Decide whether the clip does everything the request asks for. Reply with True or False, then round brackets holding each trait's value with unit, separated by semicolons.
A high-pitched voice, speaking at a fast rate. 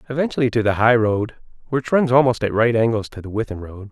False (115 Hz; 230 wpm)